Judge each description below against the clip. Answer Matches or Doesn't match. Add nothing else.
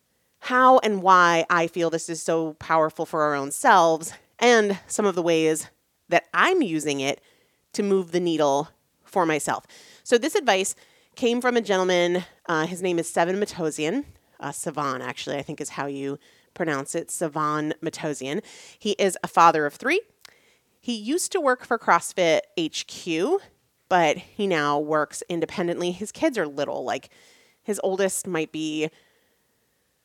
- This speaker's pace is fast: Doesn't match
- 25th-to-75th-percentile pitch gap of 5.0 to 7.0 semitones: Matches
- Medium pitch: Matches